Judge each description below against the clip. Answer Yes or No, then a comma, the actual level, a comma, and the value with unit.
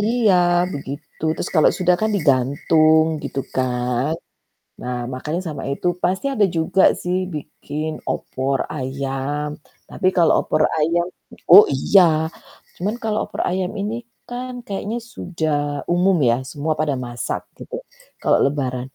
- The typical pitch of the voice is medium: Yes, medium, 155 Hz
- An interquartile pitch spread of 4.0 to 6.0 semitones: Yes, average, 5.2 semitones